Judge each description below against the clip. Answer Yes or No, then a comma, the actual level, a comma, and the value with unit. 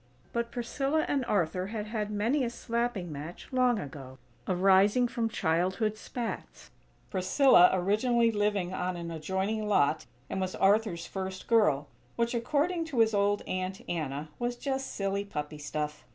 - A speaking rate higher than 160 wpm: No, average, 150 wpm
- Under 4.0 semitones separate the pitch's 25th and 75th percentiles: No, average, 4.7 semitones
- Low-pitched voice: No, high, 205 Hz